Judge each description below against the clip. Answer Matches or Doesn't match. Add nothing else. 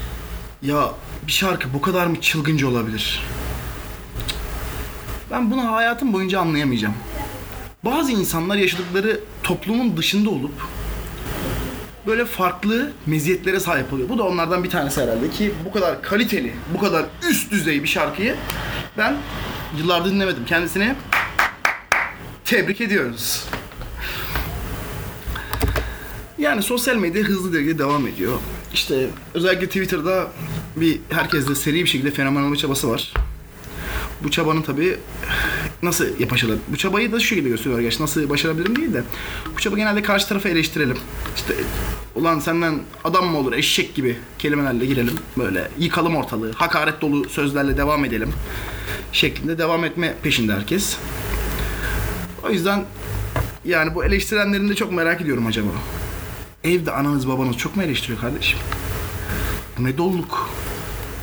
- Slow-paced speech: Doesn't match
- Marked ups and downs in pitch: Matches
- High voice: Doesn't match